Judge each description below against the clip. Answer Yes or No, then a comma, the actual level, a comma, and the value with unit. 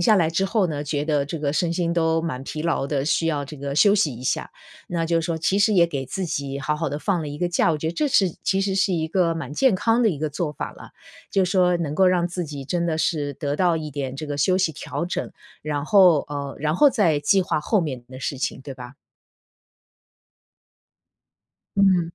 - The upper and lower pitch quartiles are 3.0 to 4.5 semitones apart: Yes, average, 3.9 semitones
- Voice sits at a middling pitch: Yes, medium, 160 Hz